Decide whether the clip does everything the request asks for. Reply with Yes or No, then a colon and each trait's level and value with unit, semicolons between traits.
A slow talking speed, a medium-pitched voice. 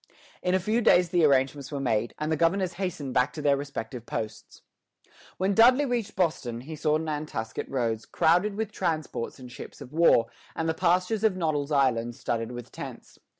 No: average, 185 wpm; medium, 155 Hz